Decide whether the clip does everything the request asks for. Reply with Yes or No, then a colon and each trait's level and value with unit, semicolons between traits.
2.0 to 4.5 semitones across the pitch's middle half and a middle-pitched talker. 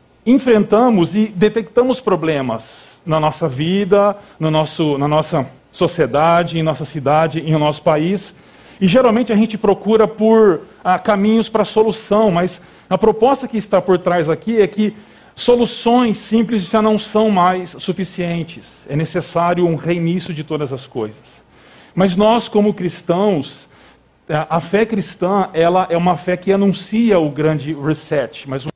No: average, 5.2 semitones; medium, 180 Hz